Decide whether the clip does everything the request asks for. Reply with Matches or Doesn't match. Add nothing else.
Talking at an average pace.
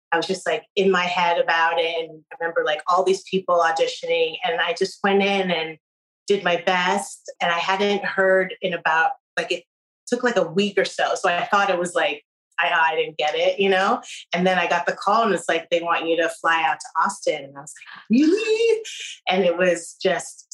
Doesn't match